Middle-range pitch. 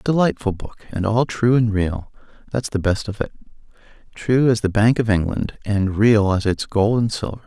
No: low, 110 Hz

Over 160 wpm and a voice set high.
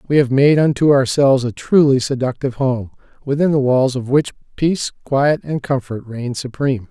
No: average, 175 wpm; low, 135 Hz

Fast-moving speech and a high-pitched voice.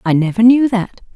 Yes: fast, 210 wpm; high, 215 Hz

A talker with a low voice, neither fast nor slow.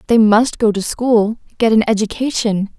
No: high, 220 Hz; average, 150 wpm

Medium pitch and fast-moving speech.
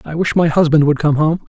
Yes: medium, 155 Hz; fast, 270 wpm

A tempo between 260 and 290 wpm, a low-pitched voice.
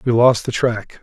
No: fast, 235 wpm; low, 115 Hz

